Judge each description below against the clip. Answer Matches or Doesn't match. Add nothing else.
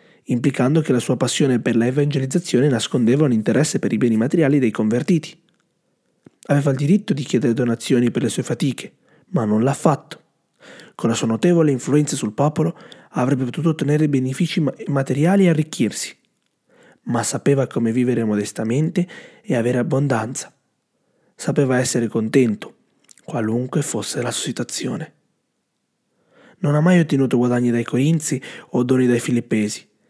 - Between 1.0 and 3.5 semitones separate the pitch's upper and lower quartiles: Doesn't match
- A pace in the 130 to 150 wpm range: Matches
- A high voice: Doesn't match